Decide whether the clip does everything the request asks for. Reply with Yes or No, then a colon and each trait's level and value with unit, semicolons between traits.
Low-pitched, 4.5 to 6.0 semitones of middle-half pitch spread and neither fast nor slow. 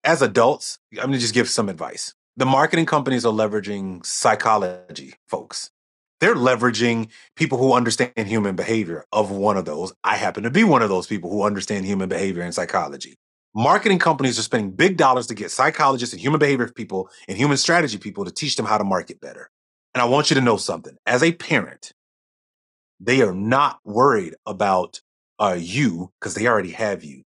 Yes: low, 115 Hz; average, 5.1 semitones; average, 190 wpm